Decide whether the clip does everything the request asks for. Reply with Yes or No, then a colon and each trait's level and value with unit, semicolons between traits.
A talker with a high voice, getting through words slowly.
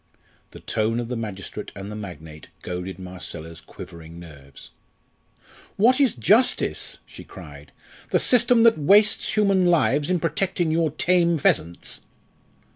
No: low, 135 Hz; slow, 130 wpm